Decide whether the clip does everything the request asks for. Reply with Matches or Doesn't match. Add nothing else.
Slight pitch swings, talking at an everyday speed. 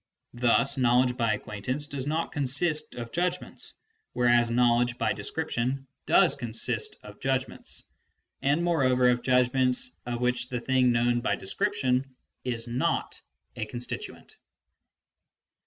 Doesn't match